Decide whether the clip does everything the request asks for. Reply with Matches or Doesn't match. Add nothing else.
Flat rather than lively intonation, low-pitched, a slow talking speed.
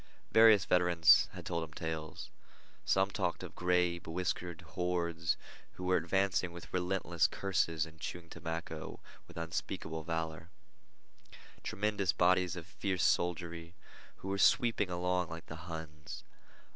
Matches